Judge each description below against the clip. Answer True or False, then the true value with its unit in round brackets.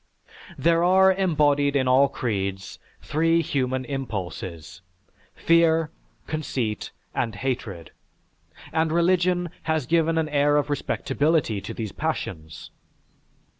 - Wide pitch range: True (5.7 semitones)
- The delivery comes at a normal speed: False (105 wpm)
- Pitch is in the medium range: True (145 Hz)